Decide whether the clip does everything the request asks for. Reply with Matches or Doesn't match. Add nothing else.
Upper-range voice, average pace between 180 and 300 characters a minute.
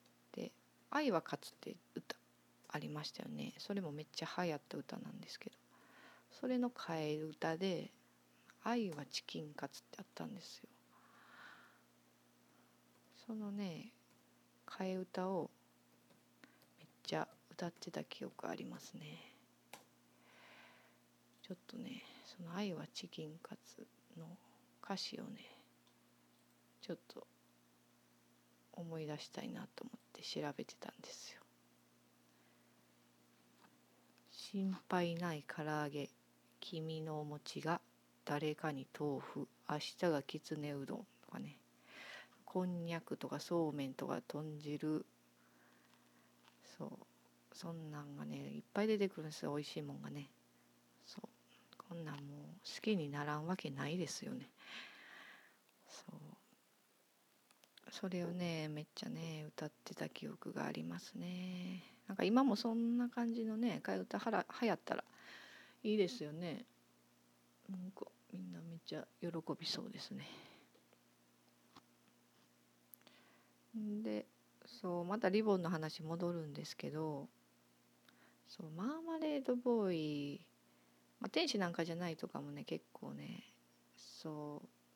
Doesn't match